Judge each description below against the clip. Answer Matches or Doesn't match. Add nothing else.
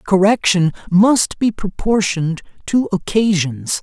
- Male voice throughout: Matches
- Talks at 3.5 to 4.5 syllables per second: Matches